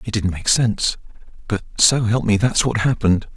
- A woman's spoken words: No, male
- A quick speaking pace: No, average, 195 wpm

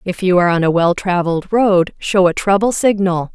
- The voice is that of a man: No, female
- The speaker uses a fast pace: Yes, fast, 215 wpm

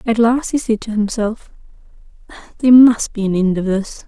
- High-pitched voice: Yes, high, 220 Hz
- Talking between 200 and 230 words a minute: No, average, 190 wpm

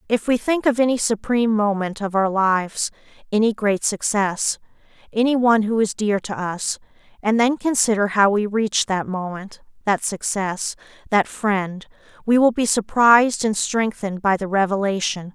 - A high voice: Yes, high, 210 Hz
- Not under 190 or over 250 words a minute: No, average, 160 wpm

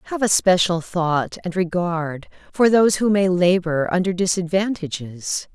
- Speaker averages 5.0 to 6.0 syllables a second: No, 4.4 syllables/s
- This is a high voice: No, medium, 180 Hz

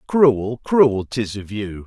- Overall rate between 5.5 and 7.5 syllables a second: No, 2.9 syllables/s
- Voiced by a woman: No, male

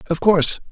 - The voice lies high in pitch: No, medium, 175 Hz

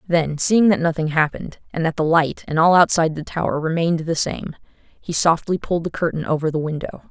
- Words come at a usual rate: No, fast, 210 wpm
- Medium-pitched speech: Yes, medium, 165 Hz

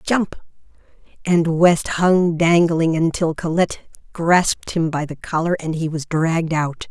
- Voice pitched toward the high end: No, medium, 165 Hz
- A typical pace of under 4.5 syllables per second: Yes, 4.2 syllables/s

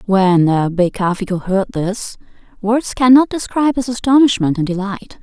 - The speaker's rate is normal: No, slow, 125 wpm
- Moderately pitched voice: No, high, 210 Hz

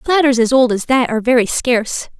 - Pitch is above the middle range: Yes, high, 245 Hz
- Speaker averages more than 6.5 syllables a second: No, 5.9 syllables/s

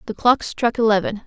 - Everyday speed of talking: Yes, average, 190 wpm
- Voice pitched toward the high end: Yes, high, 225 Hz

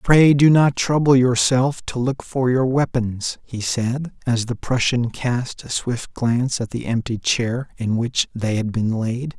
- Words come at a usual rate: Yes, average, 185 wpm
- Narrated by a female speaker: No, male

